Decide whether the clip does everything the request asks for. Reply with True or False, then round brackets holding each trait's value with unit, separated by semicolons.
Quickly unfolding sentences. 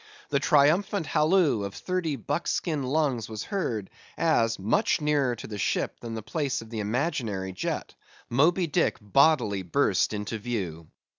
False (165 wpm)